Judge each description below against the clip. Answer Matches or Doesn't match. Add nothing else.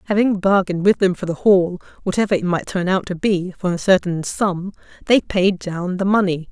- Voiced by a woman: Matches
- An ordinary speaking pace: Doesn't match